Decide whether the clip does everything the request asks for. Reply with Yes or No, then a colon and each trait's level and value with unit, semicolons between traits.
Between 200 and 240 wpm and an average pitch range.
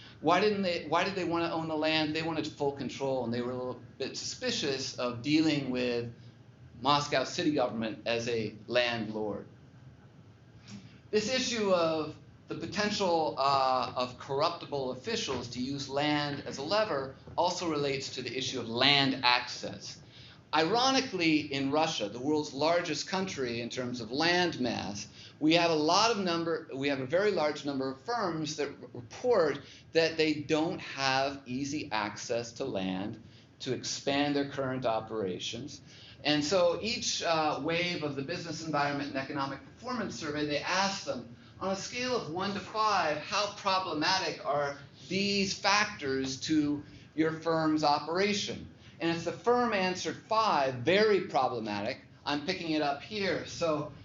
No: average, 155 wpm; average, 4.8 semitones